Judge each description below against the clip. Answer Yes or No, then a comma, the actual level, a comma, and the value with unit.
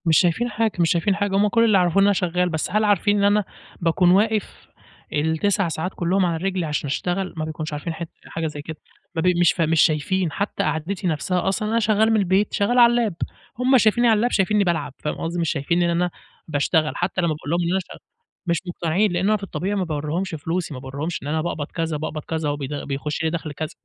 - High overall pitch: No, medium, 175 Hz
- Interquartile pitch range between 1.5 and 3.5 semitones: No, average, 4.1 semitones